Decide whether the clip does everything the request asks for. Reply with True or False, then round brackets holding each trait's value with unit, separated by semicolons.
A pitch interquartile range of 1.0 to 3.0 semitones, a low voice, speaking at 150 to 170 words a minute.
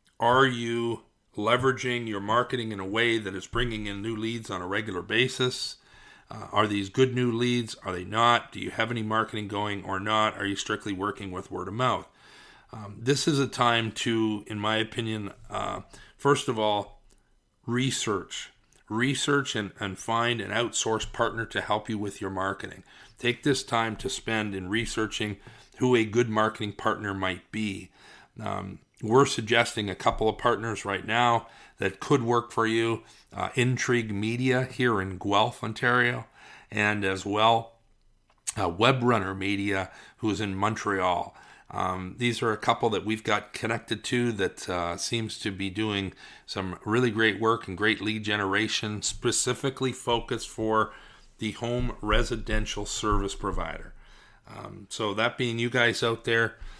True (2.6 semitones; 110 Hz; 165 wpm)